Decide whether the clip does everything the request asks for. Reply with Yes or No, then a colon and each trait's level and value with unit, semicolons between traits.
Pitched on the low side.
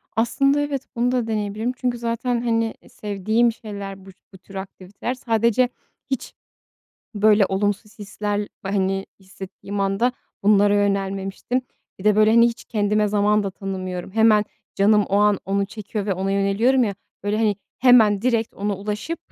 No: high, 210 Hz